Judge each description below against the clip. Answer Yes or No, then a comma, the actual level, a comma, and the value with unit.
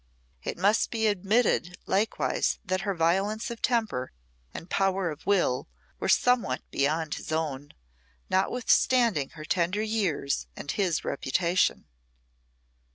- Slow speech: Yes, slow, 120 wpm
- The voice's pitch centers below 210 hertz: Yes, medium, 185 Hz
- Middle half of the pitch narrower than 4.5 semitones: No, average, 5.3 semitones